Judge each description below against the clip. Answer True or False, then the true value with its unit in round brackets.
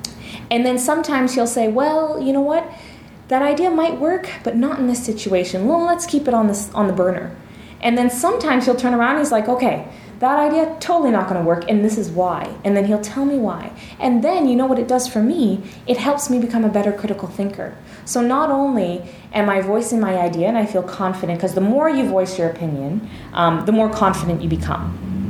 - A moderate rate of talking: False (225 wpm)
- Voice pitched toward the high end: True (225 Hz)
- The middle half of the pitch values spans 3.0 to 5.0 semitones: False (5.6 semitones)